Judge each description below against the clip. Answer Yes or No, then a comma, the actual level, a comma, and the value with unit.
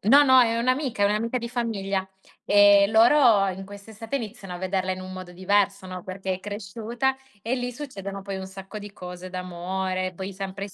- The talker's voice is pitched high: Yes, high, 200 Hz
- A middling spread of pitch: Yes, average, 3.4 semitones